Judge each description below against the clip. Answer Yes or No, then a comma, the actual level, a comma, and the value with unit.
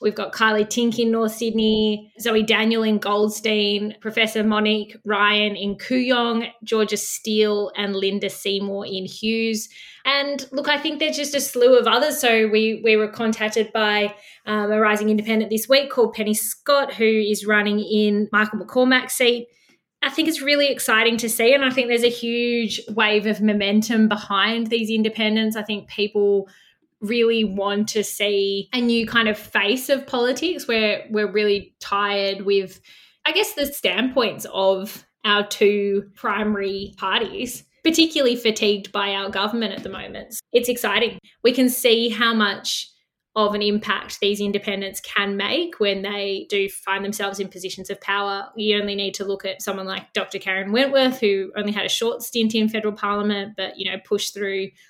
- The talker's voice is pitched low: No, high, 215 Hz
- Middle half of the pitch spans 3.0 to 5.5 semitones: No, narrow, 2.4 semitones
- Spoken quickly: No, average, 175 wpm